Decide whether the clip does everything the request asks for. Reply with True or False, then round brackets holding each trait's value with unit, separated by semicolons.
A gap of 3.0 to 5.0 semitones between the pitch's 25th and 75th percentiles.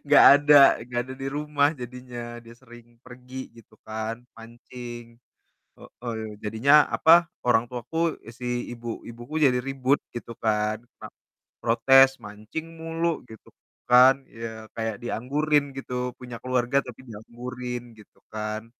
False (2.6 semitones)